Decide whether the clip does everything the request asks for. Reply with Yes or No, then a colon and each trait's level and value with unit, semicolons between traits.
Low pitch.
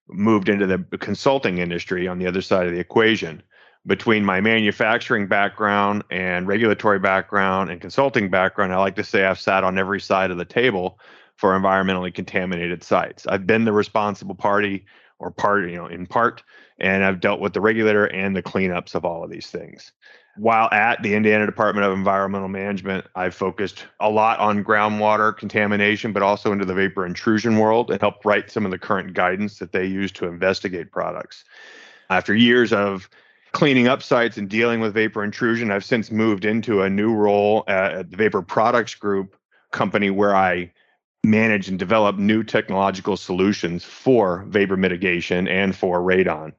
Yes: low, 100 Hz